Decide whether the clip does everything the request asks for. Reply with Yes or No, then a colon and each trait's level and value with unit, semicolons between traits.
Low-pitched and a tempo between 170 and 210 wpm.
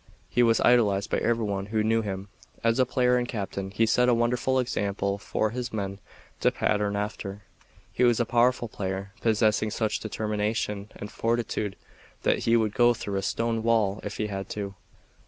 Yes: low, 110 Hz; average, 185 wpm